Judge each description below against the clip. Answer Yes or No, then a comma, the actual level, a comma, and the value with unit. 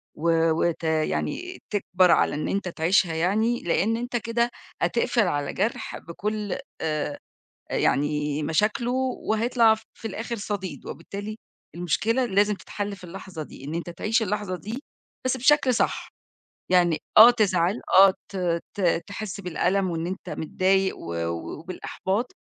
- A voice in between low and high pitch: No, high, 195 Hz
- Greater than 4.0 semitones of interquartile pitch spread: Yes, average, 4.5 semitones